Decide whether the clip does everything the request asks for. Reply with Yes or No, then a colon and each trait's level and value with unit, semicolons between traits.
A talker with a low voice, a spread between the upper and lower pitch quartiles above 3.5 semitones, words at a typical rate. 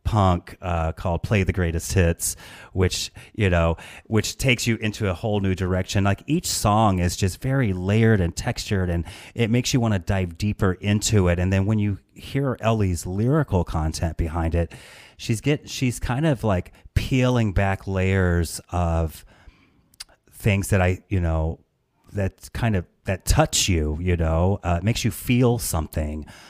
Yes: very low, 95 Hz; average, 4.2 semitones; average, 170 wpm